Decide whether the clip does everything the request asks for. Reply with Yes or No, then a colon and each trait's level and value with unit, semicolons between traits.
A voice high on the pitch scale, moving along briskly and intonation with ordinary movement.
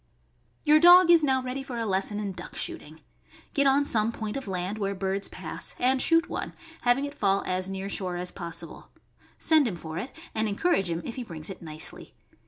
No: high, 210 Hz; fast, 210 wpm; wide, 6.5 semitones